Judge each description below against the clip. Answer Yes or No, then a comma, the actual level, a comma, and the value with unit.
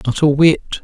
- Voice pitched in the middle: Yes, medium, 150 Hz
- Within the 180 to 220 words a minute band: Yes, fast, 215 wpm